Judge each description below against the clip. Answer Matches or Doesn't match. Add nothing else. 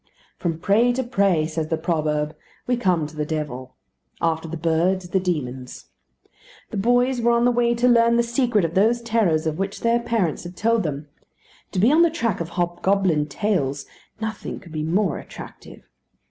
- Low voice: Doesn't match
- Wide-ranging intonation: Matches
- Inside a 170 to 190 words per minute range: Matches